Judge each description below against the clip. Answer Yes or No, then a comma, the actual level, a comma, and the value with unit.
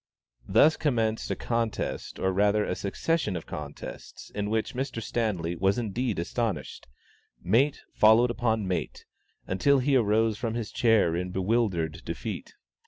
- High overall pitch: No, low, 110 Hz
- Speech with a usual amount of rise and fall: Yes, average, 4.0 semitones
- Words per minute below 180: Yes, average, 140 wpm